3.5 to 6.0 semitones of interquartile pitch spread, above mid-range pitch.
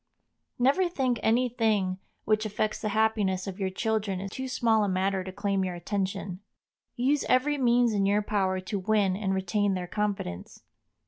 No: average, 2.9 semitones; high, 205 Hz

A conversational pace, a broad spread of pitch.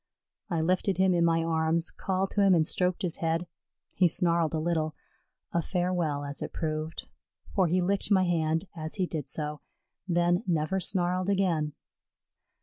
No: average, 165 wpm; narrow, 2.5 semitones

